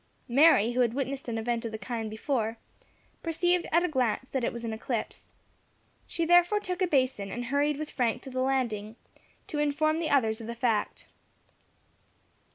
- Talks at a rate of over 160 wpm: Yes, average, 180 wpm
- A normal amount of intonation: Yes, average, 5.0 semitones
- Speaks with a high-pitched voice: Yes, very high, 255 Hz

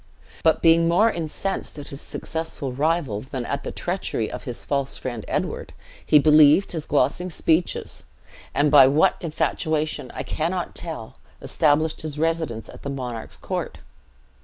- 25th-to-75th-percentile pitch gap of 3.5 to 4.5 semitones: No, average, 3.0 semitones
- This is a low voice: No, medium, 155 Hz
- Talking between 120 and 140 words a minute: No, average, 150 wpm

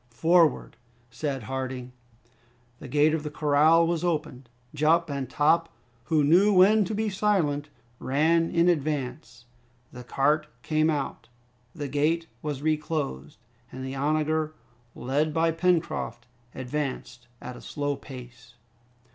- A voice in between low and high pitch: Yes, medium, 150 Hz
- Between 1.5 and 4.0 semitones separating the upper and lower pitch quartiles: Yes, average, 3.5 semitones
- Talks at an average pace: No, slow, 130 wpm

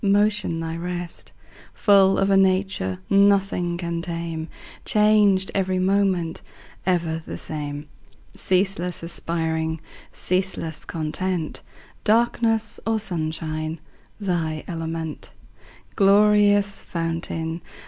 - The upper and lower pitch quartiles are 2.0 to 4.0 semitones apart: Yes, average, 3.3 semitones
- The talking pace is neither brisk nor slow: No, slow, 90 wpm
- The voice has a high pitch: No, medium, 180 Hz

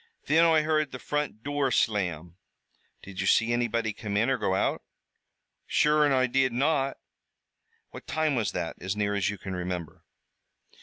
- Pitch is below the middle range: Yes, low, 120 Hz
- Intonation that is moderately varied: No, wide, 6.8 semitones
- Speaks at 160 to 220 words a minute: Yes, average, 170 wpm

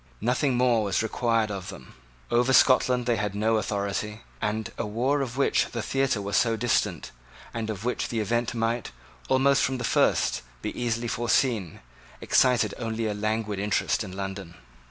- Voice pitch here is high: No, low, 115 Hz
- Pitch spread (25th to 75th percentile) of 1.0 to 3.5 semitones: Yes, average, 2.7 semitones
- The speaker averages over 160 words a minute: Yes, average, 170 wpm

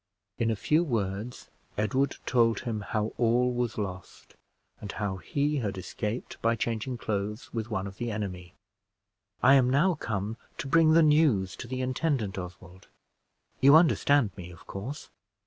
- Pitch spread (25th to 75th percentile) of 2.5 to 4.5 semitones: No, average, 4.9 semitones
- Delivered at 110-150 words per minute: No, average, 160 wpm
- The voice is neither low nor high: No, low, 115 Hz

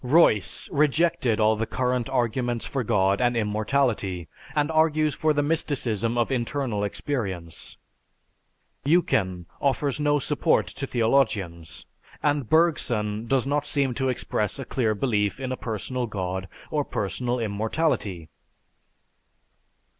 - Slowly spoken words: Yes, slow, 125 wpm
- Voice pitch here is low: Yes, low, 120 Hz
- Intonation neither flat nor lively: Yes, average, 5.0 semitones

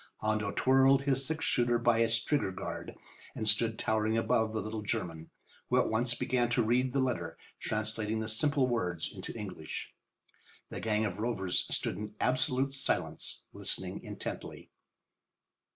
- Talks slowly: No, average, 150 wpm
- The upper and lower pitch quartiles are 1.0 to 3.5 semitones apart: Yes, average, 2.9 semitones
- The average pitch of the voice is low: Yes, low, 115 Hz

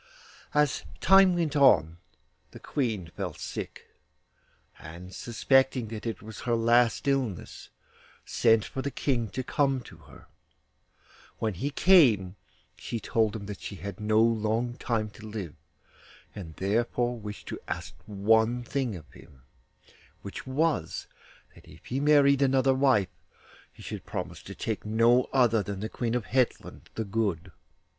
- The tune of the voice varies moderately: Yes, average, 4.1 semitones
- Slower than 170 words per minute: Yes, average, 150 wpm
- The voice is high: No, low, 115 Hz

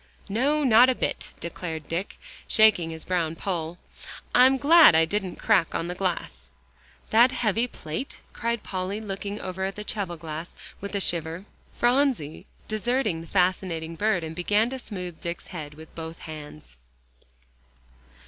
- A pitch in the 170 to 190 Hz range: Yes, medium, 185 Hz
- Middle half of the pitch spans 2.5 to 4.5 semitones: No, average, 5.1 semitones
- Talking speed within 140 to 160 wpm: Yes, average, 150 wpm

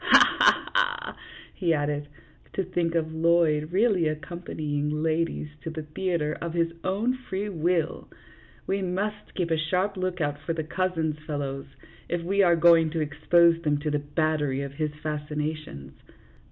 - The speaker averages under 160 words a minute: No, average, 165 wpm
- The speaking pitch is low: No, medium, 165 Hz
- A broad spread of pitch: No, average, 3.0 semitones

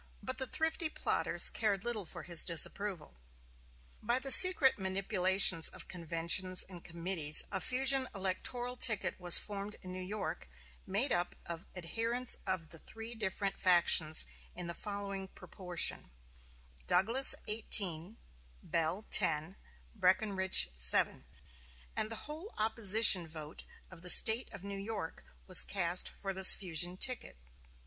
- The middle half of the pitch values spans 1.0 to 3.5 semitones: No, average, 4.1 semitones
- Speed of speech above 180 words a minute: No, slow, 135 wpm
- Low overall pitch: No, high, 190 Hz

